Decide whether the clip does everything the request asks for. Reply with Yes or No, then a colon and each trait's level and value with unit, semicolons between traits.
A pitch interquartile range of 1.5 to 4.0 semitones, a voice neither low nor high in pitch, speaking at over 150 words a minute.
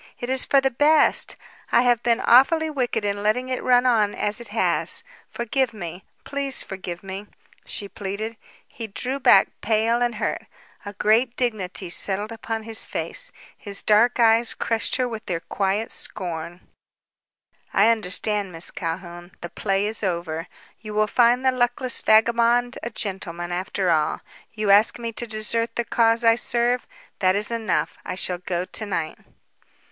No: average, 3.6 semitones; high, 220 Hz; average, 165 wpm